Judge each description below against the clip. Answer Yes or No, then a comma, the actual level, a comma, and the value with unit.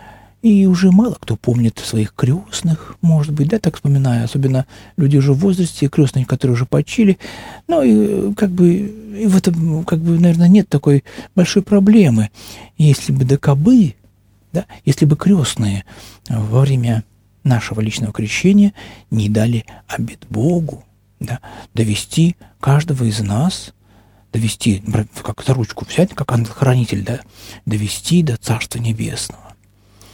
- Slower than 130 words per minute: No, average, 135 wpm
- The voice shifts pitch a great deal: Yes, wide, 7.7 semitones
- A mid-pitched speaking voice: No, low, 130 Hz